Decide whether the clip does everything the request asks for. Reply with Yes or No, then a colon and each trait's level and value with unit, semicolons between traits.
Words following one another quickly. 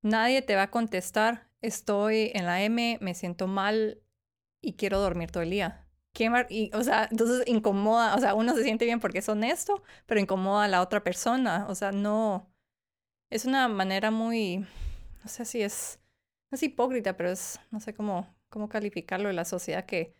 No: average, 190 wpm